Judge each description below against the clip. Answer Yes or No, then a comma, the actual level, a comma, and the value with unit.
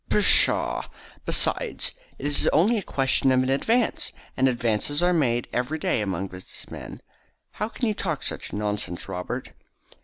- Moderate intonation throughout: No, wide, 7.6 semitones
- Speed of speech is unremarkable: Yes, average, 155 wpm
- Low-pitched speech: Yes, low, 130 Hz